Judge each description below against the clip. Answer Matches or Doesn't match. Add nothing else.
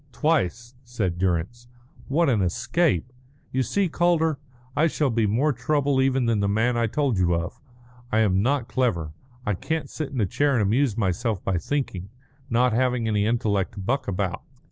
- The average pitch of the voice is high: Doesn't match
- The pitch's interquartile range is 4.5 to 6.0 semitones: Matches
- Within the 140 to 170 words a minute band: Doesn't match